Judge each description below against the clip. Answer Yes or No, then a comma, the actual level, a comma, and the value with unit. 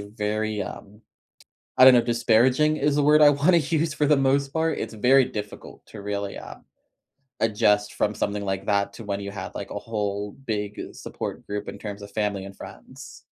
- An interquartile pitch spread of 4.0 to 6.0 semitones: Yes, average, 5.0 semitones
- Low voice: Yes, low, 110 Hz